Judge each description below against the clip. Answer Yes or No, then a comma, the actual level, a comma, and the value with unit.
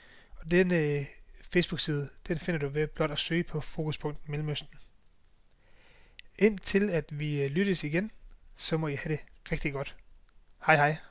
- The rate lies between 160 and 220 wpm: No, average, 150 wpm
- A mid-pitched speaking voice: Yes, medium, 155 Hz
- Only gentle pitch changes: No, average, 3.1 semitones